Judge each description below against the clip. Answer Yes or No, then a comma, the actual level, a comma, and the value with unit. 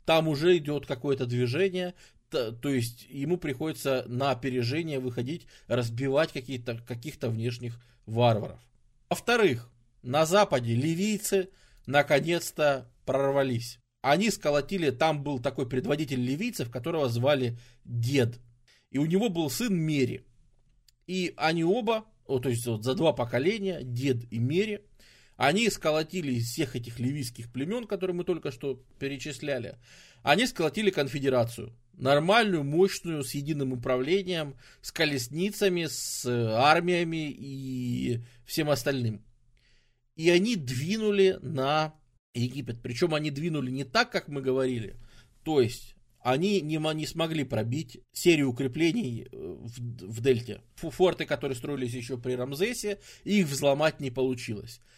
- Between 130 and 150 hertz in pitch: Yes, medium, 140 Hz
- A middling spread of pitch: Yes, average, 4.8 semitones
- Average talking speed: No, slow, 120 wpm